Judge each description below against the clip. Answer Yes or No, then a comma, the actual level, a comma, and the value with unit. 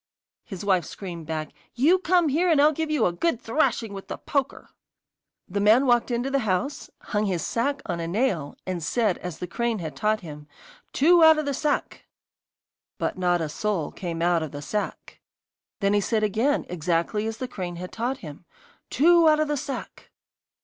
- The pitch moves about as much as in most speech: No, wide, 7.8 semitones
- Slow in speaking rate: No, average, 195 wpm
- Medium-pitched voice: No, high, 215 Hz